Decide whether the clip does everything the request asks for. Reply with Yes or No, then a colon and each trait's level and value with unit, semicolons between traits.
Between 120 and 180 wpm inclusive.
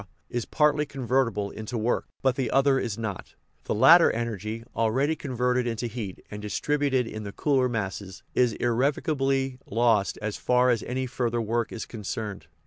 Yes: average, 165 wpm